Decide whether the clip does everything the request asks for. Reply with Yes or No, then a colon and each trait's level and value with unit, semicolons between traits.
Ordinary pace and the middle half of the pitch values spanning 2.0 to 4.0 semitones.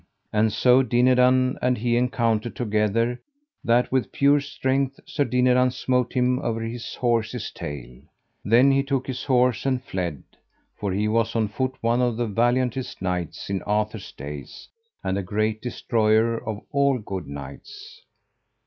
Yes: average, 150 wpm; average, 3.1 semitones